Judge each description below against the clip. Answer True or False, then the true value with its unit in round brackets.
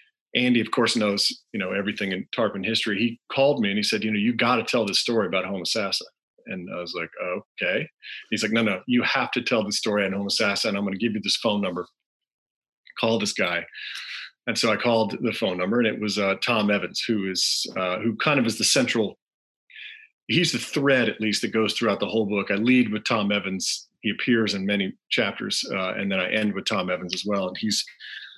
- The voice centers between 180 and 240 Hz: False (110 Hz)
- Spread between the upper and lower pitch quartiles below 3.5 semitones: True (2.9 semitones)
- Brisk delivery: True (235 wpm)